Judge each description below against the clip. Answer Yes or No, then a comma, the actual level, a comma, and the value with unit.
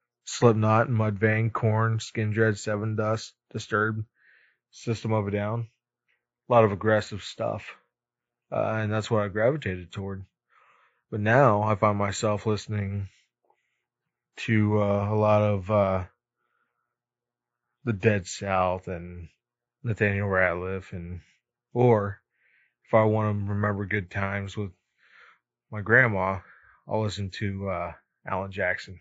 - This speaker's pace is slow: Yes, slow, 130 wpm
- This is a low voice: Yes, low, 105 Hz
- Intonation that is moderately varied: No, narrow, 2.2 semitones